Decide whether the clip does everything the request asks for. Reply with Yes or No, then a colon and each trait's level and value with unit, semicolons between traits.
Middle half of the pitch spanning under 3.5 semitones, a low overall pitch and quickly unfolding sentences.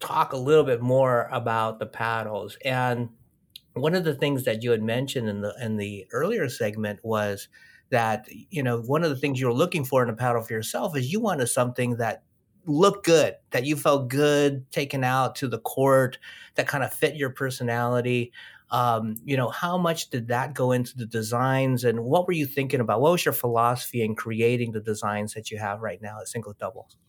No: average, 3.8 semitones; low, 125 Hz; fast, 210 wpm